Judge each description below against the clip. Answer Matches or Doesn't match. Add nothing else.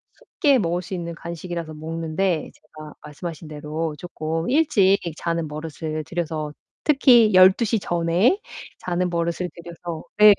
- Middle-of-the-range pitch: Matches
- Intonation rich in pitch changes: Doesn't match